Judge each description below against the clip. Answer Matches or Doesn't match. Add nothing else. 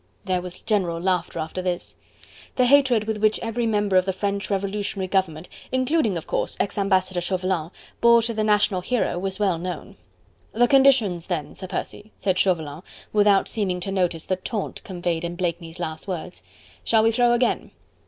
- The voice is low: Doesn't match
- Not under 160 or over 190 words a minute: Matches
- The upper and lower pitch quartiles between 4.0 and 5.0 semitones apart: Doesn't match